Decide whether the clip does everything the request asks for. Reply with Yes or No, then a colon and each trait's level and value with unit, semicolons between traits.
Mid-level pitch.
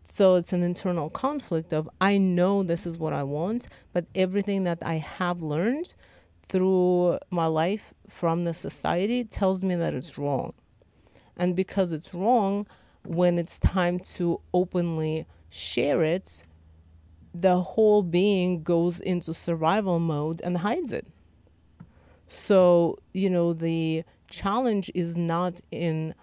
Yes: medium, 175 Hz